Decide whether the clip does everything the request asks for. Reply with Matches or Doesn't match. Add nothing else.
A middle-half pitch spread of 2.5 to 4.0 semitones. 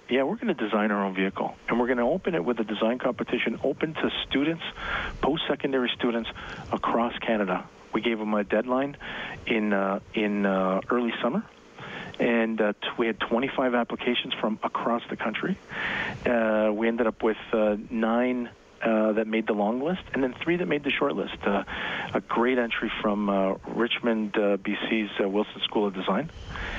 Matches